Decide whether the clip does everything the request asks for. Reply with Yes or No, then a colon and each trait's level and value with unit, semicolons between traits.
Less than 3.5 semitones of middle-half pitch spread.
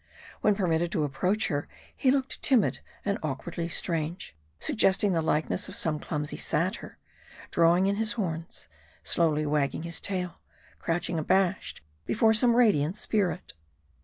No: average, 4.1 semitones